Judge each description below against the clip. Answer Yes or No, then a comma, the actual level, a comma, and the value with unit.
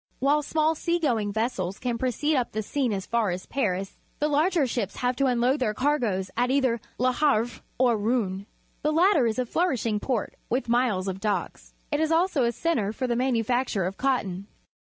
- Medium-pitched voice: No, high, 245 Hz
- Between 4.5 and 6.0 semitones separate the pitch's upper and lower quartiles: Yes, average, 4.8 semitones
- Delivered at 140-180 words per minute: No, average, 195 wpm